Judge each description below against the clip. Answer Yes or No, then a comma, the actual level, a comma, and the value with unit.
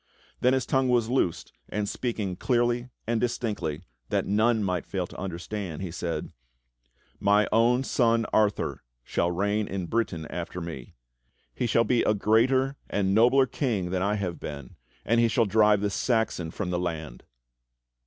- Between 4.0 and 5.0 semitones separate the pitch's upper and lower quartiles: Yes, average, 4.6 semitones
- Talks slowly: No, average, 165 wpm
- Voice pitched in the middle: No, low, 105 Hz